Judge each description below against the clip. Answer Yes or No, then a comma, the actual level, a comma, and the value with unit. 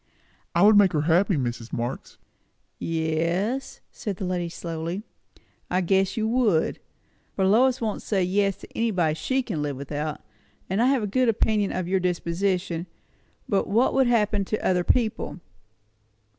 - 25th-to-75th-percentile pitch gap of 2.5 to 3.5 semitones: No, average, 4.4 semitones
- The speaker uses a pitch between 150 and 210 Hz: Yes, high, 190 Hz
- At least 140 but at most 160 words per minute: Yes, average, 155 wpm